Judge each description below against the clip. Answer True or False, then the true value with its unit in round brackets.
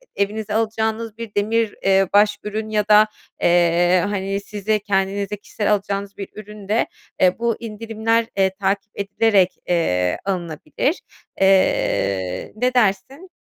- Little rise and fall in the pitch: True (2.3 semitones)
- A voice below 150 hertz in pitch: False (205 Hz)